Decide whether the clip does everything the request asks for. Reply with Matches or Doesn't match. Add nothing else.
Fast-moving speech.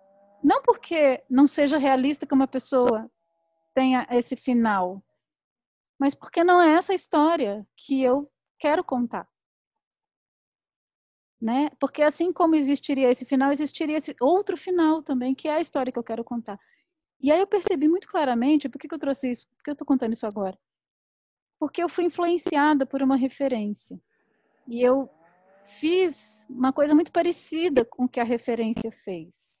Doesn't match